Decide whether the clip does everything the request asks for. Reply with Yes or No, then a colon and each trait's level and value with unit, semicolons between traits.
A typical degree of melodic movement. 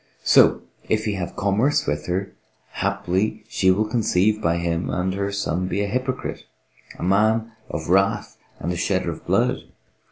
Yes: average, 3.3 semitones